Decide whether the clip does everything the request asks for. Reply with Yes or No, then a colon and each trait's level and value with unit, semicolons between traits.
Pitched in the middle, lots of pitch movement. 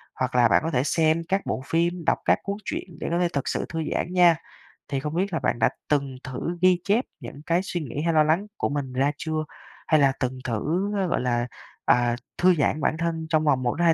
No: medium, 155 Hz; average, 4.2 semitones